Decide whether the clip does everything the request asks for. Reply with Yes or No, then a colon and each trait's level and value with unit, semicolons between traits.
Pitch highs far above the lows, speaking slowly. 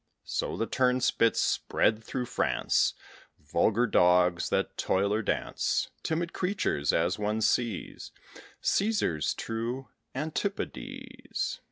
Yes: wide, 8.5 semitones; slow, 100 wpm